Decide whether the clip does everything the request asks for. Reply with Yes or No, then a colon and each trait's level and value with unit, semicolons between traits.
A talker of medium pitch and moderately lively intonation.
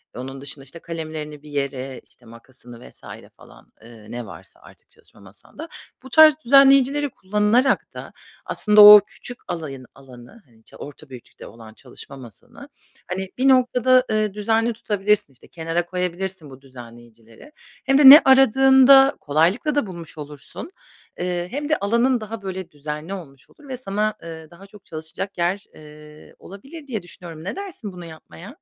No: medium, 180 Hz; wide, 8.9 semitones